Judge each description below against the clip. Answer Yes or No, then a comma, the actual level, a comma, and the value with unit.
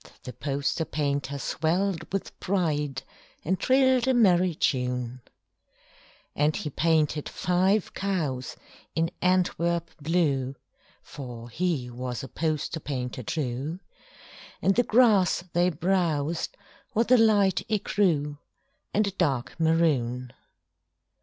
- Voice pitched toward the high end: No, medium, 160 Hz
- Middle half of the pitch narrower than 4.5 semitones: No, average, 5.2 semitones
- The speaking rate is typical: No, slow, 115 wpm